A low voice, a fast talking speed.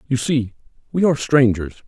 No: low, 125 Hz; average, 160 wpm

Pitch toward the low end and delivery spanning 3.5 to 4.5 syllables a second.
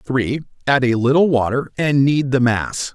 Yes: low, 130 Hz; 4.3 syllables/s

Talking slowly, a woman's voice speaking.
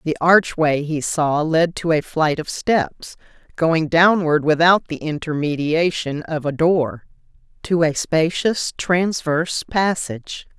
Yes: slow, 130 wpm; female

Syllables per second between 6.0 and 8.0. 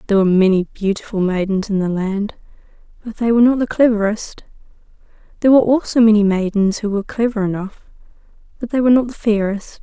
Yes: 6.6 syllables/s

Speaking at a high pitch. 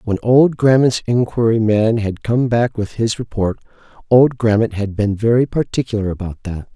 No: low, 110 Hz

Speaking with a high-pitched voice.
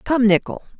Yes: high, 220 Hz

